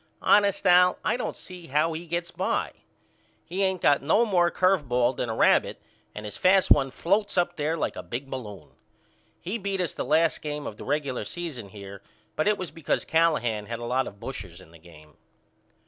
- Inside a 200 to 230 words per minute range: Yes, fast, 205 wpm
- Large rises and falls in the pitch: Yes, wide, 7.3 semitones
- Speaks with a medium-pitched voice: Yes, medium, 150 Hz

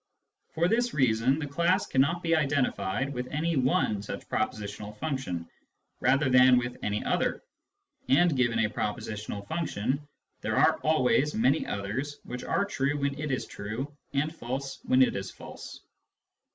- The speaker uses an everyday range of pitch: Yes, average, 4.6 semitones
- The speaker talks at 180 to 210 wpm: No, average, 160 wpm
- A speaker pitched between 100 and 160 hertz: Yes, low, 135 Hz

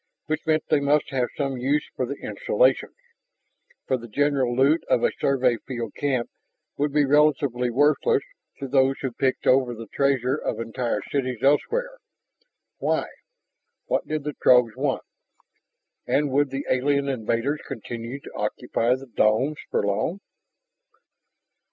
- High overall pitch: No, low, 135 Hz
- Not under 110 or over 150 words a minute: Yes, average, 145 wpm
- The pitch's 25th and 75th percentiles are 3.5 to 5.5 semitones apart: No, average, 2.9 semitones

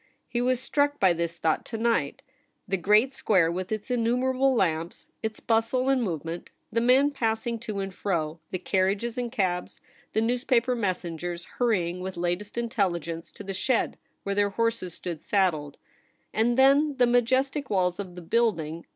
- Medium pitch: No, high, 210 Hz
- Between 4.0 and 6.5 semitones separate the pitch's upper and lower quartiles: Yes, wide, 5.4 semitones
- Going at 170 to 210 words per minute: Yes, average, 180 wpm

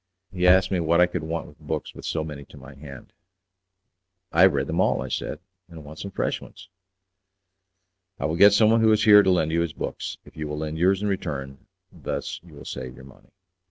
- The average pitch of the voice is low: Yes, very low, 85 Hz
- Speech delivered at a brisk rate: Yes, fast, 230 wpm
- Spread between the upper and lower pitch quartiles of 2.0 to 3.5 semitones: No, average, 4.0 semitones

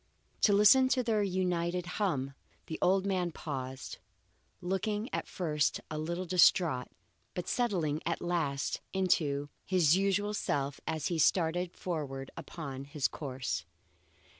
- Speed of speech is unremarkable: No, slow, 130 wpm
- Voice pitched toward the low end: No, medium, 175 Hz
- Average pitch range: Yes, average, 4.6 semitones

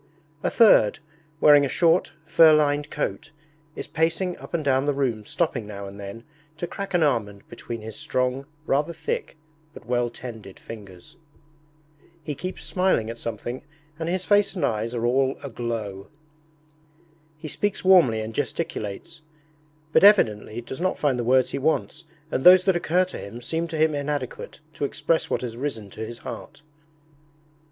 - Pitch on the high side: No, medium, 140 Hz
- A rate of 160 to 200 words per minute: Yes, average, 165 wpm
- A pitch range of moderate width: No, wide, 6.2 semitones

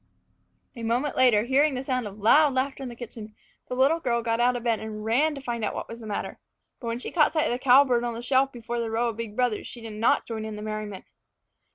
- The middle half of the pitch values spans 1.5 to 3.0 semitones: Yes, narrow, 2.6 semitones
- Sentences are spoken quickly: Yes, fast, 265 wpm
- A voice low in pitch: No, high, 240 Hz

